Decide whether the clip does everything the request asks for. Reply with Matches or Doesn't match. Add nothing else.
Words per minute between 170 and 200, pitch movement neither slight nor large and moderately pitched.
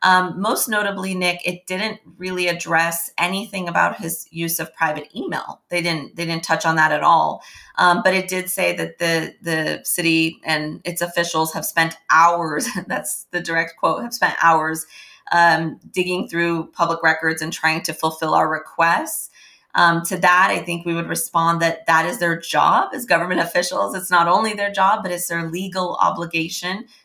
Doesn't match